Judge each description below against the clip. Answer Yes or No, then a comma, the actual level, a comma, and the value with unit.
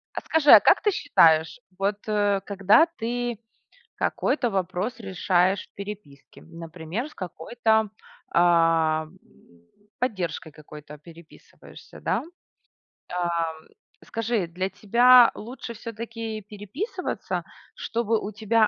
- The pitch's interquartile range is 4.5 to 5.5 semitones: Yes, average, 5.2 semitones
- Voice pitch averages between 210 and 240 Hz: No, high, 200 Hz